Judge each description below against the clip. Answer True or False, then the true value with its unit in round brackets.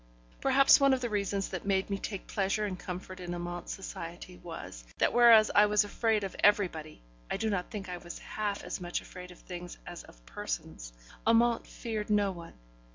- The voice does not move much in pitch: False (3.3 semitones)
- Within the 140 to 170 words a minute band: False (195 wpm)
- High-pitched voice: True (195 Hz)